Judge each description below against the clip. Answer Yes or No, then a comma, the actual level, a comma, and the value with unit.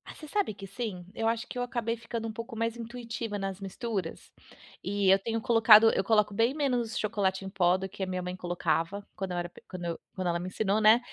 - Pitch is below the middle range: No, high, 210 Hz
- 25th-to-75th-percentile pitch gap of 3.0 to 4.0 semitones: Yes, average, 3.4 semitones